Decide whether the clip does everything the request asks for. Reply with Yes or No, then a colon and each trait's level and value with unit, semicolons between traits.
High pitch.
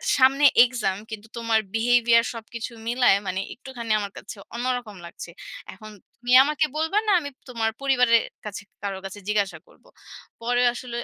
Yes: high, 235 Hz